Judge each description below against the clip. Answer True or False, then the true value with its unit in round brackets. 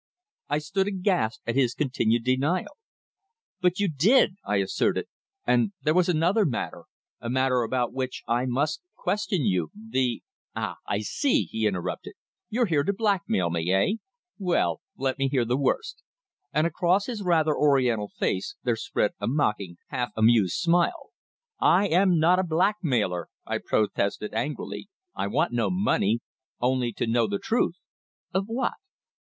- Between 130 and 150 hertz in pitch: True (140 Hz)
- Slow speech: False (155 wpm)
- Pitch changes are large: True (7.9 semitones)